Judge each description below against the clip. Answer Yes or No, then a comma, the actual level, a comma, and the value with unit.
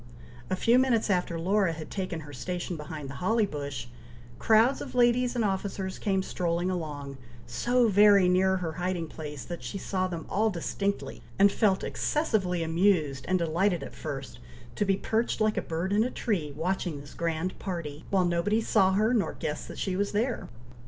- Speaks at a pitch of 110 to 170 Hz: No, medium, 185 Hz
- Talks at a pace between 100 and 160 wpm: No, average, 185 wpm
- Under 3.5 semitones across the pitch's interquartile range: No, average, 3.9 semitones